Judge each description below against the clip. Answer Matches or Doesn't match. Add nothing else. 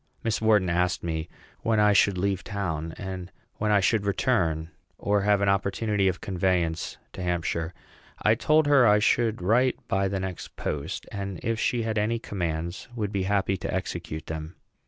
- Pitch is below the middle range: Matches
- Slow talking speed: Doesn't match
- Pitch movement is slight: Doesn't match